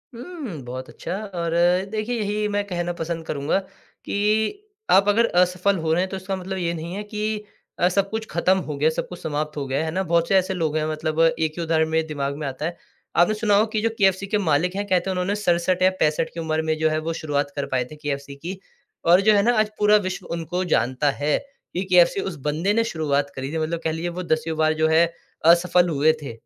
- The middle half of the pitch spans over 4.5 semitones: No, average, 3.7 semitones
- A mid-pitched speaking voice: Yes, medium, 170 Hz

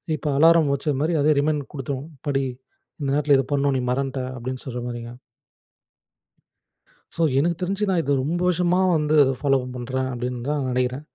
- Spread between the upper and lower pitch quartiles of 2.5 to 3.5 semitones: Yes, average, 2.9 semitones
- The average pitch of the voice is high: No, medium, 140 Hz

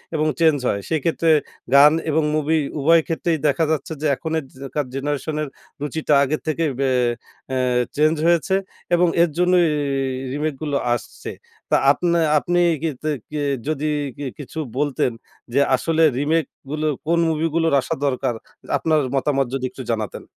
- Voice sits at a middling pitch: Yes, medium, 155 Hz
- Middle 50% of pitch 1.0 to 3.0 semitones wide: Yes, narrow, 2.5 semitones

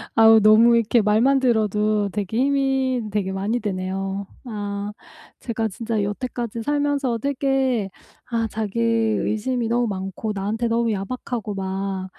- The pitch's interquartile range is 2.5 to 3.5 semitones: Yes, average, 3.0 semitones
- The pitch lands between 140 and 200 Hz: No, high, 220 Hz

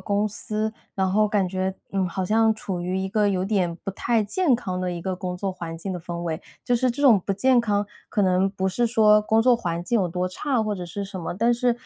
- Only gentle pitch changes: No, average, 3.2 semitones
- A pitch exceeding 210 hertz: No, high, 200 Hz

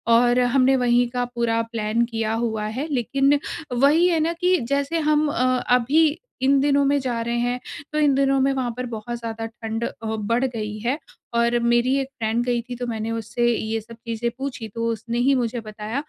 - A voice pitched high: Yes, high, 240 Hz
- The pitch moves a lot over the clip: No, average, 2.9 semitones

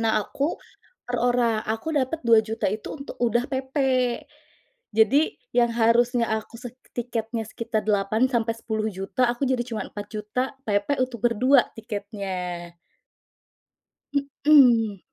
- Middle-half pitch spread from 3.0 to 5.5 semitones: No, narrow, 2.5 semitones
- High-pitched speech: Yes, high, 230 Hz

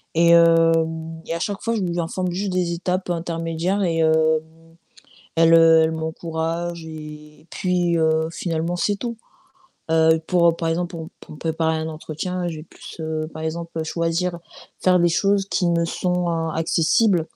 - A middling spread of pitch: No, narrow, 1.6 semitones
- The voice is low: No, medium, 165 Hz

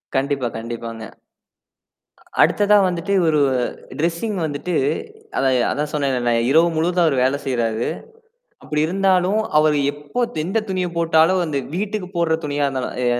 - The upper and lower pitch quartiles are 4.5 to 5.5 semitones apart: Yes, average, 4.9 semitones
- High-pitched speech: No, medium, 155 Hz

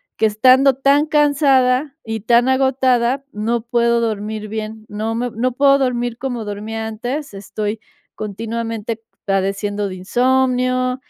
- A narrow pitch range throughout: No, average, 3.2 semitones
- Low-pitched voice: No, high, 235 Hz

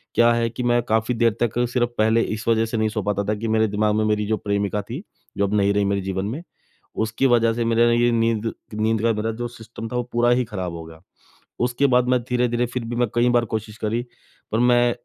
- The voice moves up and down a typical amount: No, narrow, 2.0 semitones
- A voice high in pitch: No, low, 115 Hz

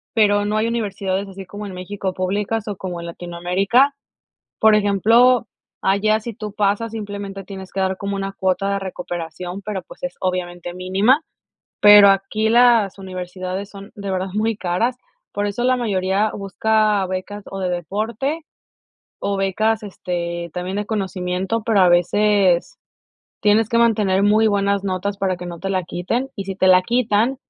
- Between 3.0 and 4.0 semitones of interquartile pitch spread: No, narrow, 2.5 semitones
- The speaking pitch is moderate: No, high, 200 Hz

